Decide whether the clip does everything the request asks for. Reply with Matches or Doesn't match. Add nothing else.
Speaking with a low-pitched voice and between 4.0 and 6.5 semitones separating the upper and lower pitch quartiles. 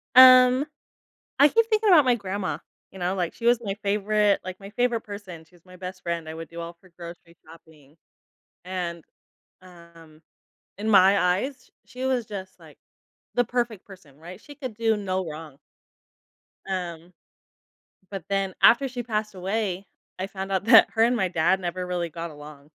Doesn't match